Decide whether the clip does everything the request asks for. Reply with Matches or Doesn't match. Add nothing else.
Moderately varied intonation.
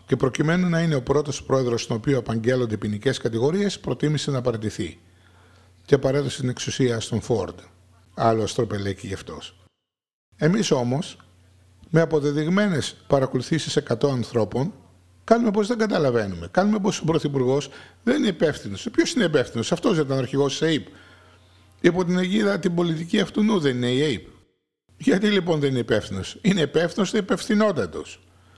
Doesn't match